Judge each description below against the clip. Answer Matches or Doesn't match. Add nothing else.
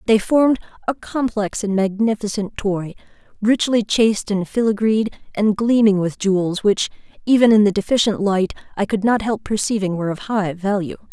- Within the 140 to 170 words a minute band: Matches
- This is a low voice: Doesn't match